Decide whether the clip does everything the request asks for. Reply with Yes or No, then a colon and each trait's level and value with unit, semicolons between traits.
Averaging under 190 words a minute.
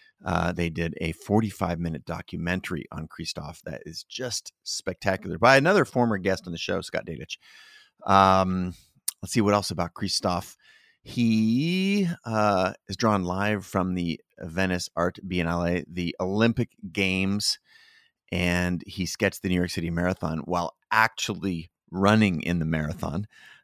Yes: average, 140 wpm